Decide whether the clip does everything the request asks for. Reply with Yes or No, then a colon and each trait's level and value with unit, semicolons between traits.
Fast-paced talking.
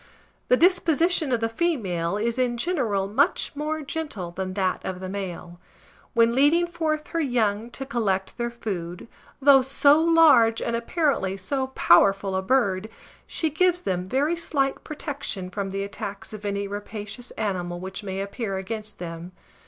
No: average, 160 wpm